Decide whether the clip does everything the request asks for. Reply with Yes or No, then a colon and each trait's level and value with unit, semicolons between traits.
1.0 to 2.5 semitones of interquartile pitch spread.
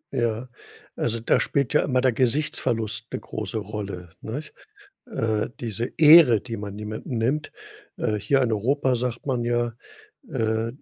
No: average, 2.9 semitones